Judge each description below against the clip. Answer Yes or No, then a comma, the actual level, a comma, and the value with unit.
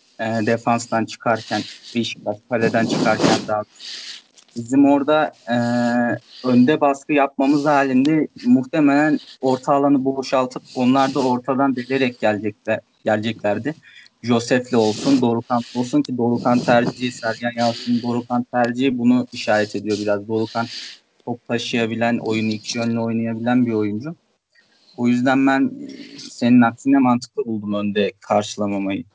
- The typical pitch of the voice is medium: No, low, 120 Hz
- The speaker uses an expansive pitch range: No, average, 3.0 semitones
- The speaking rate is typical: Yes, average, 115 wpm